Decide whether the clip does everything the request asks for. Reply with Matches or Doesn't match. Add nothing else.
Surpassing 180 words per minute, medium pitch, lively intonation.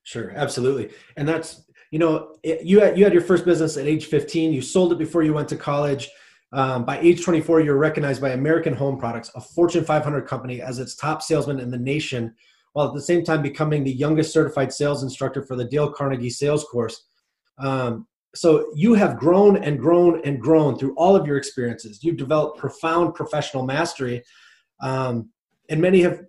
Doesn't match